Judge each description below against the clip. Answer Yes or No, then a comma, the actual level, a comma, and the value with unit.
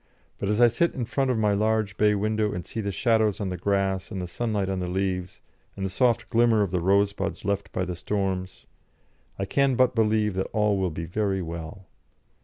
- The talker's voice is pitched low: Yes, low, 100 Hz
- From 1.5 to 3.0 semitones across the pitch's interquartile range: Yes, narrow, 2.5 semitones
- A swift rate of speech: Yes, fast, 215 wpm